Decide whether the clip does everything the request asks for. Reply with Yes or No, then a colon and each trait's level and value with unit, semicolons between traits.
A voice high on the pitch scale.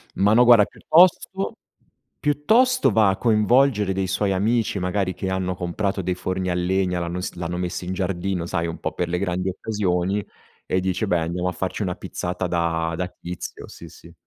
No: very low, 95 Hz